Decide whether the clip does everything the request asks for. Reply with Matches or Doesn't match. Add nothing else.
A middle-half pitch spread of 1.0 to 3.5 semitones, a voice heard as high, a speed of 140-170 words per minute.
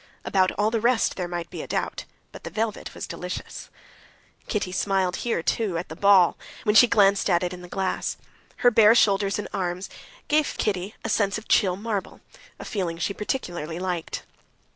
Doesn't match